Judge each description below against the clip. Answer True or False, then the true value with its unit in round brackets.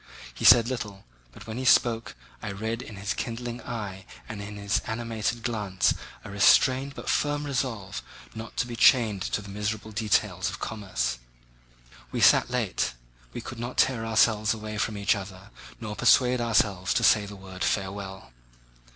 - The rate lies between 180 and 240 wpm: False (170 wpm)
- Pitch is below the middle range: True (110 Hz)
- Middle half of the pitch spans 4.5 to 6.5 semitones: False (2.6 semitones)